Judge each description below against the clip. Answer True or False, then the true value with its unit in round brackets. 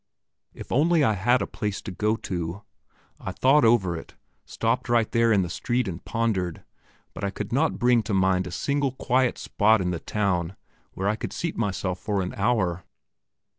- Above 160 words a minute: True (190 wpm)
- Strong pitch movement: False (4.4 semitones)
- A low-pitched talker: True (105 Hz)